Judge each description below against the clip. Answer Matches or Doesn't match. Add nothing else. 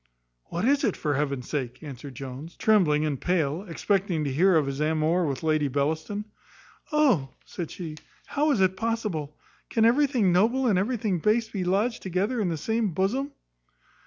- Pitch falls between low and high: Matches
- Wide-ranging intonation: Matches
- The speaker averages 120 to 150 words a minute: Doesn't match